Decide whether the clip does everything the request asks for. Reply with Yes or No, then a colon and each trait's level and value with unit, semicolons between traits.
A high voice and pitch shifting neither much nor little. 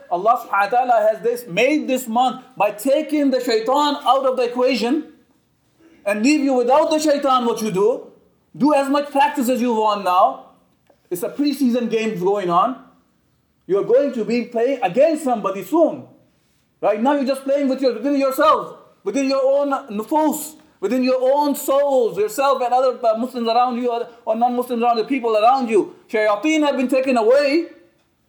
Yes: very high, 260 Hz; average, 3.5 semitones